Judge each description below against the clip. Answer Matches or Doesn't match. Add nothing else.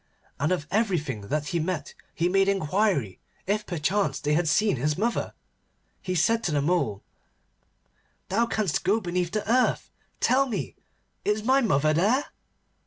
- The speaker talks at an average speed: Matches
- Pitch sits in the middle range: Matches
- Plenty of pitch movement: Matches